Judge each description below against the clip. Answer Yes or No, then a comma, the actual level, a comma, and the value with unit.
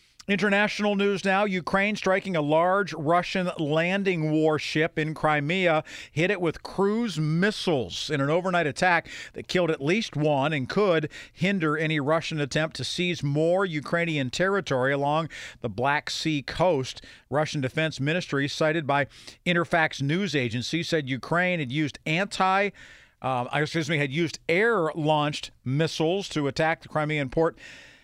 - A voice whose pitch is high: No, medium, 160 Hz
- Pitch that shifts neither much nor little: Yes, average, 3.3 semitones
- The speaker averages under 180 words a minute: Yes, average, 145 wpm